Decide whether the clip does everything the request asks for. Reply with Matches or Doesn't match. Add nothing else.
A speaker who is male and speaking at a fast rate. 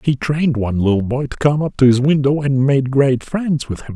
Matches